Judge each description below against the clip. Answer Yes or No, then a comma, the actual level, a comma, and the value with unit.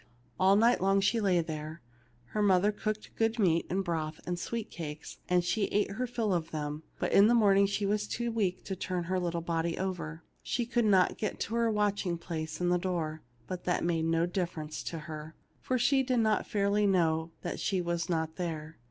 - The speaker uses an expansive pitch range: No, average, 4.1 semitones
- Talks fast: Yes, fast, 215 wpm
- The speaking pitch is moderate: Yes, medium, 180 Hz